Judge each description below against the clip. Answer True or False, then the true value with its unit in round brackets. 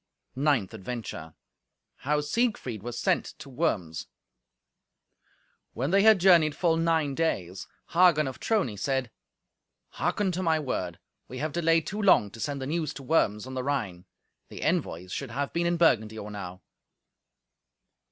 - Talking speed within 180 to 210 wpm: False (150 wpm)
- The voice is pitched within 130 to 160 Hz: True (140 Hz)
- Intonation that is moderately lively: False (7.3 semitones)